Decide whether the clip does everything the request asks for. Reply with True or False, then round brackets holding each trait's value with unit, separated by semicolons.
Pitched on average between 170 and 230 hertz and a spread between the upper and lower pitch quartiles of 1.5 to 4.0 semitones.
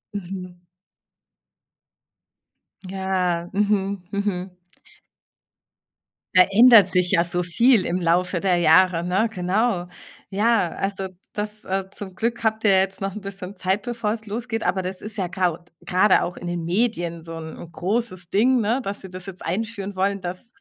True (190 Hz; 2.7 semitones)